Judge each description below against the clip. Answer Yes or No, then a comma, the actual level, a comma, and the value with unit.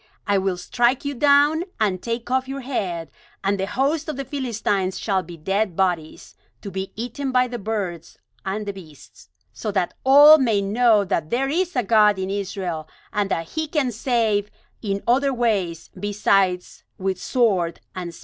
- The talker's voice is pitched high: Yes, high, 205 Hz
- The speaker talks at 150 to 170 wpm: No, average, 180 wpm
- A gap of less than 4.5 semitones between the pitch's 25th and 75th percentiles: No, average, 5.0 semitones